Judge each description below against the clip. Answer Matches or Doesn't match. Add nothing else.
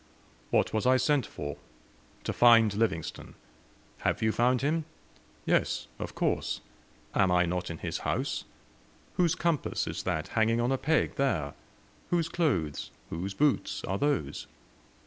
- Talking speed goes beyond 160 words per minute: Doesn't match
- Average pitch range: Doesn't match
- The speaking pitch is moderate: Doesn't match